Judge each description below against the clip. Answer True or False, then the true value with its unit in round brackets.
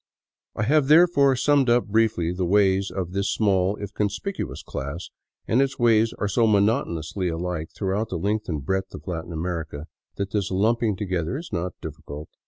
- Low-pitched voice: True (100 Hz)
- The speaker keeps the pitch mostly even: False (4.2 semitones)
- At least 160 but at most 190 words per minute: True (180 wpm)